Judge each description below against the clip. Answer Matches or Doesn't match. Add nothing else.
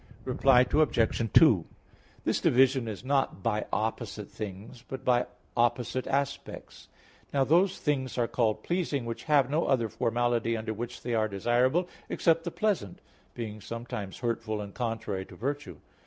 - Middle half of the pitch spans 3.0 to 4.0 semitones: Matches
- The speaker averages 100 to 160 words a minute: Matches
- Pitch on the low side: Matches